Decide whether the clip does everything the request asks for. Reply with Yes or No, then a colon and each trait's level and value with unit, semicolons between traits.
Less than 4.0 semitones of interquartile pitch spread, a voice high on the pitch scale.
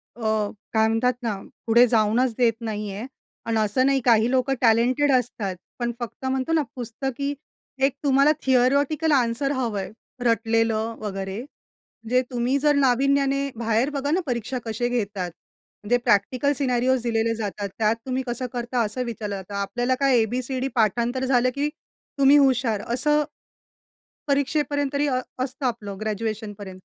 Yes: average, 3.3 semitones; high, 245 Hz